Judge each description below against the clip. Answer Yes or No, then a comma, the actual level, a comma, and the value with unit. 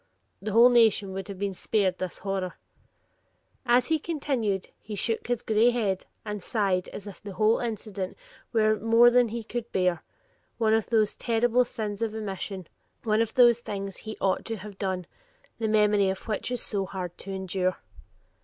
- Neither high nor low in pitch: No, high, 210 Hz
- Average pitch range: Yes, average, 3.0 semitones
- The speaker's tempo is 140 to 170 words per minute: No, average, 180 wpm